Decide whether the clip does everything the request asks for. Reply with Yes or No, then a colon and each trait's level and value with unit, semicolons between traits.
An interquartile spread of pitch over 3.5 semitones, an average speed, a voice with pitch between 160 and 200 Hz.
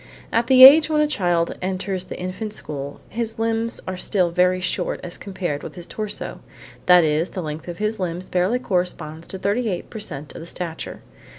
Yes: average, 4.1 semitones; average, 195 wpm; medium, 185 Hz